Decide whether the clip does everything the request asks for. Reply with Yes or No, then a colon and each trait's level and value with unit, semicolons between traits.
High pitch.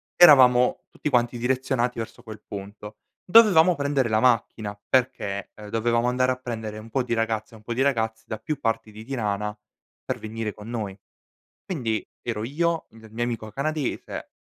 No: low, 115 Hz